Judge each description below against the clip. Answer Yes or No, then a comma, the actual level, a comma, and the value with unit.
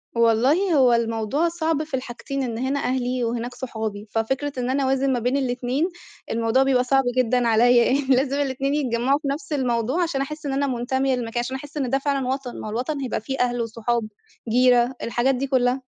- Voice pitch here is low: No, very high, 255 Hz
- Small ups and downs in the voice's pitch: Yes, narrow, 2.3 semitones